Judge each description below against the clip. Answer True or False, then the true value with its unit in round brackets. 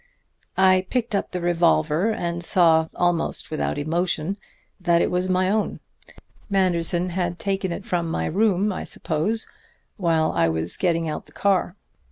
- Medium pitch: True (175 Hz)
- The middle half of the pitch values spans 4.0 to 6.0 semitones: False (2.5 semitones)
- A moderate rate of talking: True (155 wpm)